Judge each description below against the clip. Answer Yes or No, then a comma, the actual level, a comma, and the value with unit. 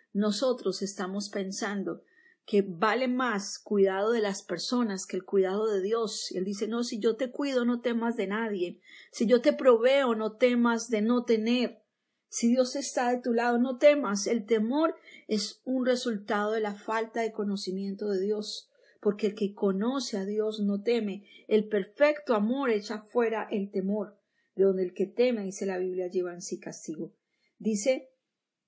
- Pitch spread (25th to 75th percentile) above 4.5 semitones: No, average, 3.3 semitones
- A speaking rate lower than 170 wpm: No, average, 175 wpm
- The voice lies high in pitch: Yes, high, 215 Hz